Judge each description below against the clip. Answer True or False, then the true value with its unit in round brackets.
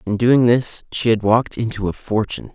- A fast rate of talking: True (210 wpm)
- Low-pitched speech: True (110 Hz)